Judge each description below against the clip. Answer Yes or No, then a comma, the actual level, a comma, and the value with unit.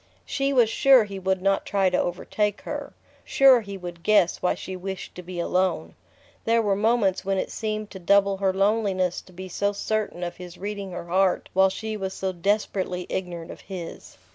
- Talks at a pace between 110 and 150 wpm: No, average, 195 wpm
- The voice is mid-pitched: No, high, 195 Hz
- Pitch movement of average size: No, narrow, 2.3 semitones